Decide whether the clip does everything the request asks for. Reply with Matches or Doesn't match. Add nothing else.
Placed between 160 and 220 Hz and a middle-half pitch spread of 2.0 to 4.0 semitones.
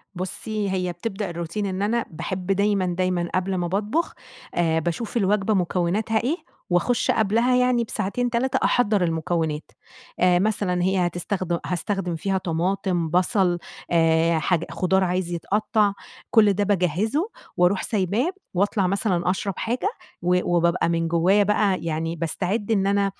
Matches